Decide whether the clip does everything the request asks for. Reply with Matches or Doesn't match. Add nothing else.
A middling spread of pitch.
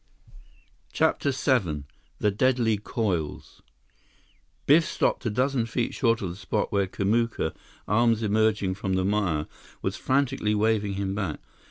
Matches